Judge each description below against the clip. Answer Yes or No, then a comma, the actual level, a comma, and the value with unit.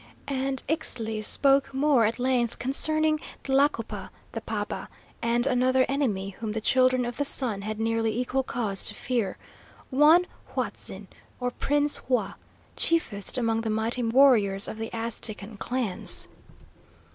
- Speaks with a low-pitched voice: No, high, 245 Hz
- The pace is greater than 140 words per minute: No, slow, 135 wpm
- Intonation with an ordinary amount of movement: Yes, average, 3.3 semitones